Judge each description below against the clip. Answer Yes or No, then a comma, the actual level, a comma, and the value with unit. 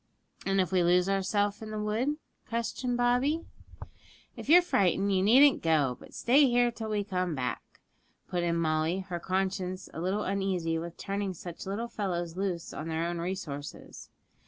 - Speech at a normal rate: Yes, average, 170 wpm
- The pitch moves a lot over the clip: No, average, 3.9 semitones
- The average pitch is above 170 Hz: Yes, high, 190 Hz